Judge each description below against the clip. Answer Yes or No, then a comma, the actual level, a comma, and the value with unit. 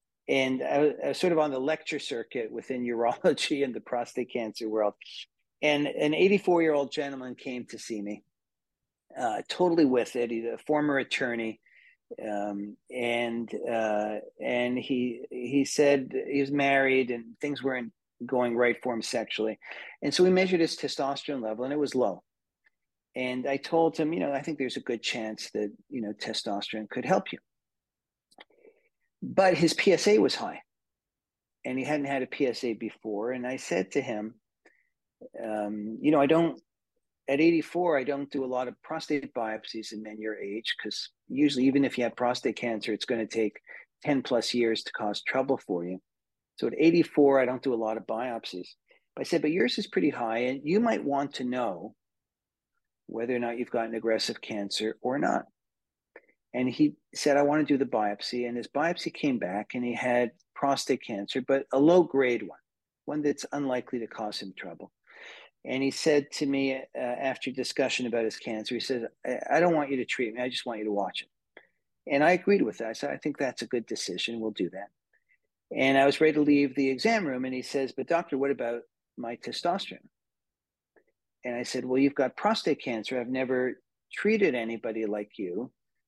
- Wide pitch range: No, average, 3.8 semitones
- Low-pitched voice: Yes, low, 125 Hz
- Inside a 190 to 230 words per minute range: Yes, average, 195 wpm